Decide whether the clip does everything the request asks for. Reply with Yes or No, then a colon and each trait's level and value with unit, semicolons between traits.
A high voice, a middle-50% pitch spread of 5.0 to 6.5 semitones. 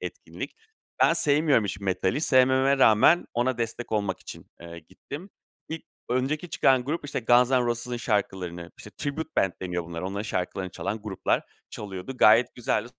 No: low, 115 Hz; wide, 5.6 semitones